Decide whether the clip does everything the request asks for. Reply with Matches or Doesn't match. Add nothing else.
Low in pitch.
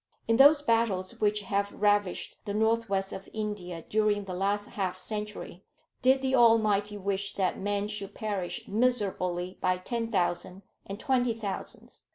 Doesn't match